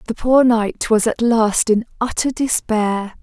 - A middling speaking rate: Yes, average, 170 wpm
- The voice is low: No, high, 225 Hz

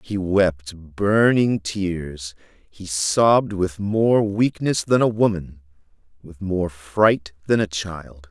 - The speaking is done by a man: Yes, male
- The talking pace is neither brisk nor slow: No, slow, 130 wpm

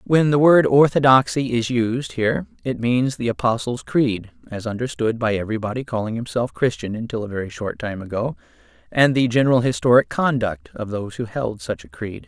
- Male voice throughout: Yes, male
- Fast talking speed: No, average, 180 wpm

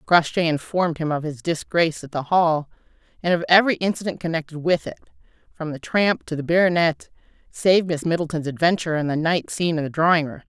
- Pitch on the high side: No, medium, 165 Hz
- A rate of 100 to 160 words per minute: No, average, 195 wpm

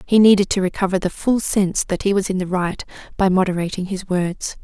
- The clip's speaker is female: Yes, female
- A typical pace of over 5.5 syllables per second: Yes, 5.8 syllables/s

